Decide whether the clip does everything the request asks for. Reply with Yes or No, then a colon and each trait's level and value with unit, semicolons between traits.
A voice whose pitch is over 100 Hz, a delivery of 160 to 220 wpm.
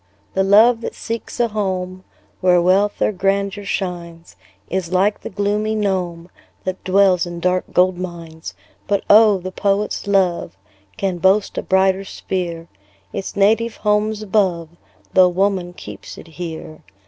No: high, 190 Hz; average, 145 wpm